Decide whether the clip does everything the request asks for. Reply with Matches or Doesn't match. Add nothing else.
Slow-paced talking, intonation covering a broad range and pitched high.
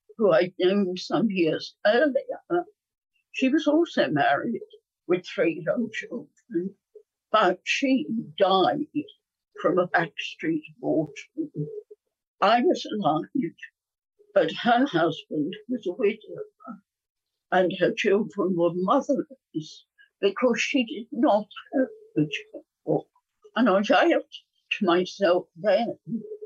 Matches